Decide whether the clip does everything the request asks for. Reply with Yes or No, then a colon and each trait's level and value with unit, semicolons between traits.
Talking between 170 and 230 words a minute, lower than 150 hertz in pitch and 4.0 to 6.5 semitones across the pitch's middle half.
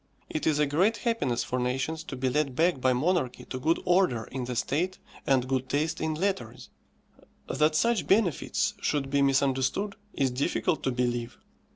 Yes: average, 175 wpm; medium, 140 Hz; average, 4.7 semitones